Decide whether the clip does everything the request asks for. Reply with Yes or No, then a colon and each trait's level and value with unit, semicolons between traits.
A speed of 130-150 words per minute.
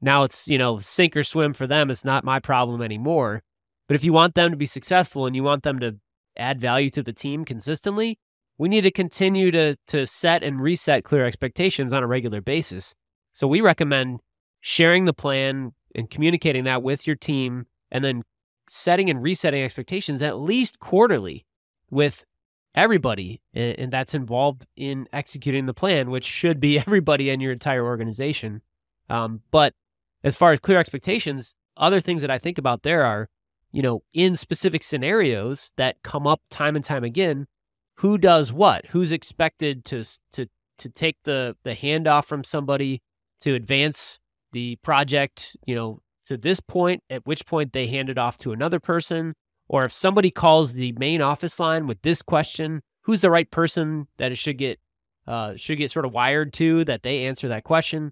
No: average, 185 wpm